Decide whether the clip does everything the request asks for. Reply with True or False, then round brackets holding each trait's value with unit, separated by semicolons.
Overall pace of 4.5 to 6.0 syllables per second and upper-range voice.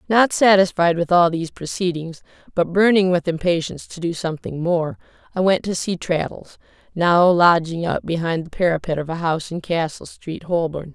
False (5.2 syllables/s; 170 Hz)